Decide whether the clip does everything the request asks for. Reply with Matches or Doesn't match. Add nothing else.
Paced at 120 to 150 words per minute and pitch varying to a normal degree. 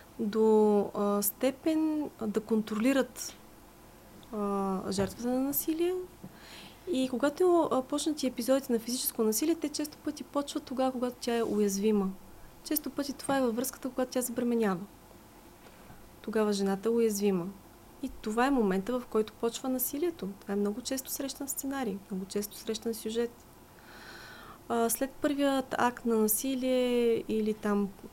Matches